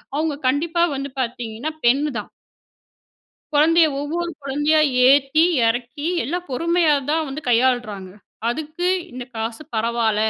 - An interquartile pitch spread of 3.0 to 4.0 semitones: No, average, 4.7 semitones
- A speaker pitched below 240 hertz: No, very high, 280 Hz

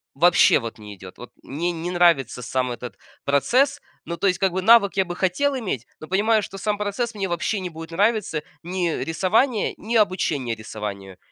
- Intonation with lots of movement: Yes, wide, 7.2 semitones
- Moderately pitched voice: Yes, medium, 175 Hz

